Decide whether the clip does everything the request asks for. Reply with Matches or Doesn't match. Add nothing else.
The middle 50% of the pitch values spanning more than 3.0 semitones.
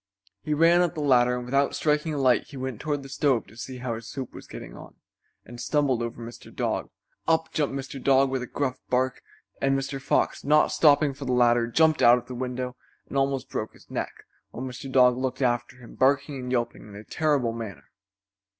Doesn't match